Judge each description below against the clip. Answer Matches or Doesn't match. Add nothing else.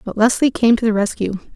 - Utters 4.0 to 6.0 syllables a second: Matches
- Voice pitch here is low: Doesn't match